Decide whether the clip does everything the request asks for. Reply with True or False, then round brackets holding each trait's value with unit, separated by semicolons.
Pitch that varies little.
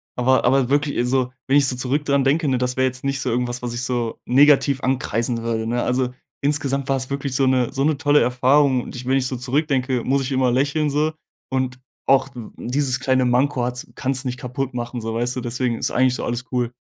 True (1.9 semitones)